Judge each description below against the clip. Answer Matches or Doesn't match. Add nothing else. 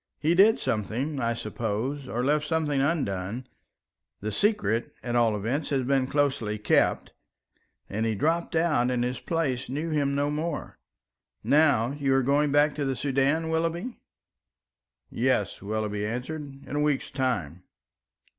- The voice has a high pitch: Doesn't match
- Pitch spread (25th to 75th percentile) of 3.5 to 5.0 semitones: Matches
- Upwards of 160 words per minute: Doesn't match